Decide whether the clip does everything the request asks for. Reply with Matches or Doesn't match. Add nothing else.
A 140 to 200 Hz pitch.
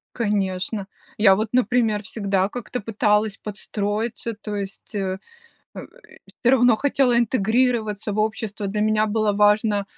Doesn't match